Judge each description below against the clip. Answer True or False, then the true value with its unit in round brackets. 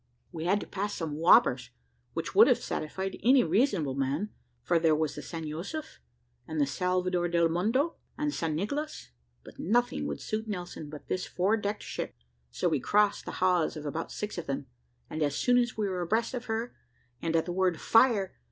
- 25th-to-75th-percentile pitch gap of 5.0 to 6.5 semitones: True (5.3 semitones)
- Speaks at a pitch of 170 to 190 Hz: True (185 Hz)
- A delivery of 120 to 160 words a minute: False (195 wpm)